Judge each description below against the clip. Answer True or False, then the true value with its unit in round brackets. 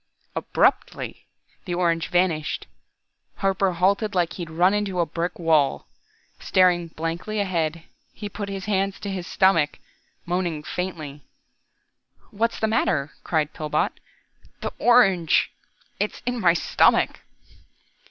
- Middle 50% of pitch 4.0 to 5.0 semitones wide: False (3.2 semitones)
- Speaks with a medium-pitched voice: True (180 Hz)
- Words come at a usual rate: False (120 wpm)